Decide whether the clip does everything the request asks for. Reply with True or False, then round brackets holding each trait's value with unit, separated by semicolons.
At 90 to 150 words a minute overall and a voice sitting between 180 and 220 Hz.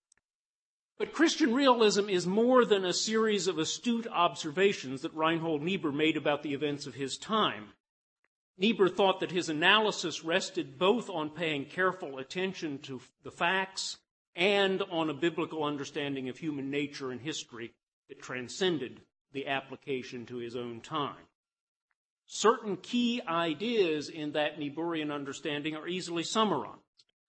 False (140 wpm; 165 Hz)